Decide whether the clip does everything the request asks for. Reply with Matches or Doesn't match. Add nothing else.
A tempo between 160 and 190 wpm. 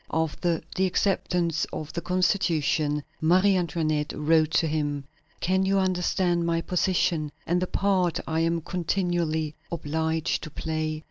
Doesn't match